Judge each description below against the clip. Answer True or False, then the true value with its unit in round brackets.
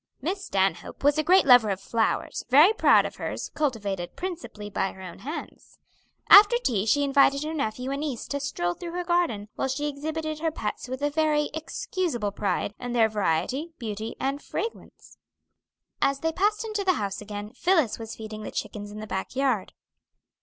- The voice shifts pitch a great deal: True (7.0 semitones)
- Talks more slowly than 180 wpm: False (190 wpm)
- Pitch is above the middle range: True (275 Hz)